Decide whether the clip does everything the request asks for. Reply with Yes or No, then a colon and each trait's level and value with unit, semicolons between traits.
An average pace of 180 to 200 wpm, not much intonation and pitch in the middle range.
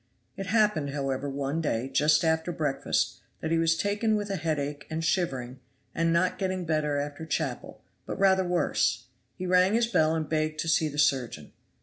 No: average, 185 wpm; average, 4.0 semitones; medium, 160 Hz